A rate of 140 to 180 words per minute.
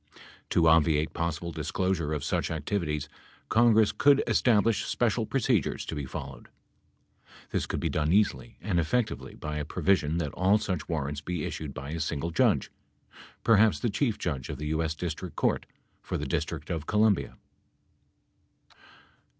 Yes: average, 155 wpm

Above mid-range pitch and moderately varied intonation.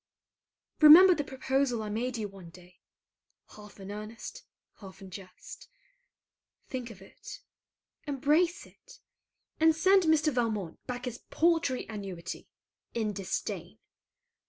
No: high, 240 Hz; wide, 7.1 semitones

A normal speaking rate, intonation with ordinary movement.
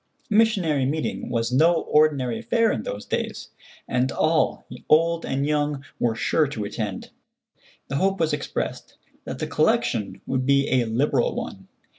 Yes: average, 155 wpm; average, 4.2 semitones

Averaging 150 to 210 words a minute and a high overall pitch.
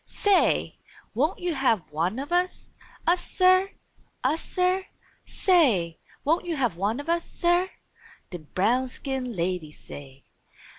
No: slow, 135 wpm; very high, 270 Hz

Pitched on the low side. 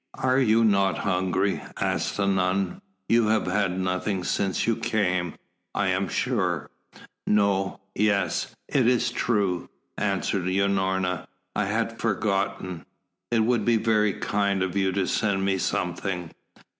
Yes: low, 100 Hz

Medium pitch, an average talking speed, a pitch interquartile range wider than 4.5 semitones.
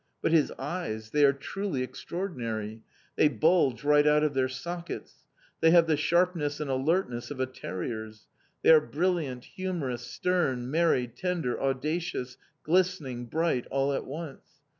Yes: medium, 145 Hz; average, 145 wpm; average, 5.0 semitones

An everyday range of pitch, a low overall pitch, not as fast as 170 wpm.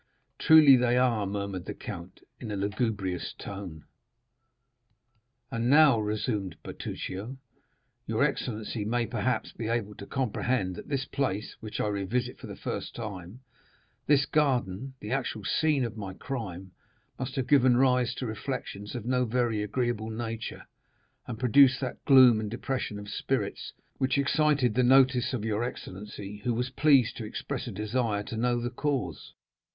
Yes: average, 3.7 semitones; low, 120 Hz; average, 150 wpm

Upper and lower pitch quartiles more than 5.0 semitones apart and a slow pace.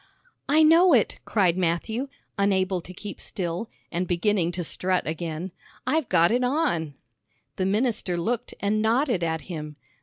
No: wide, 5.5 semitones; average, 155 wpm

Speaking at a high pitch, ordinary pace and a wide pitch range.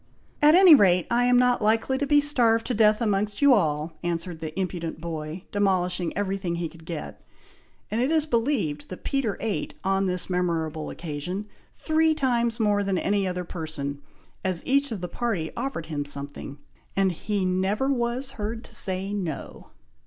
Yes: high, 195 Hz; average, 175 wpm; wide, 5.8 semitones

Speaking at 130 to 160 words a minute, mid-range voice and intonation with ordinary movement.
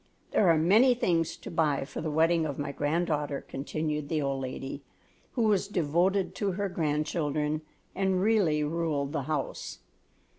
Yes: average, 155 wpm; medium, 155 Hz; average, 3.6 semitones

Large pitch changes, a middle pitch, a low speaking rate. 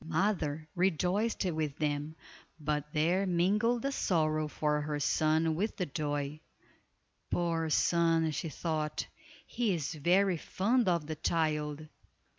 No: average, 3.0 semitones; medium, 160 Hz; slow, 130 wpm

